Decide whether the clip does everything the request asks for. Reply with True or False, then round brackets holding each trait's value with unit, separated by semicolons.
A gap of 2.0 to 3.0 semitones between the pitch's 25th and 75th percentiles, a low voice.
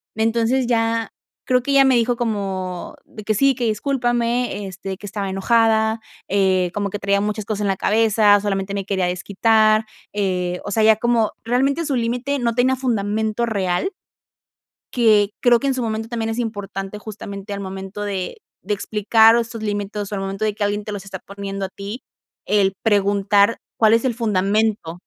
False (2.6 semitones; 215 Hz)